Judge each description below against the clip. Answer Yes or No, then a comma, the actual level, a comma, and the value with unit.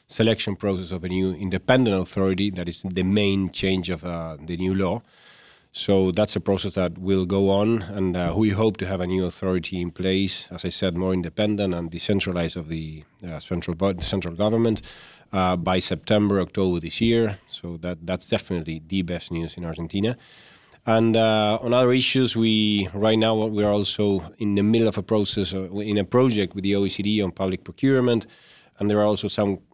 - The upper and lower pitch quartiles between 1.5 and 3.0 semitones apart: Yes, narrow, 2.6 semitones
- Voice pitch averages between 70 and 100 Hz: Yes, very low, 95 Hz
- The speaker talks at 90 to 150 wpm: No, average, 190 wpm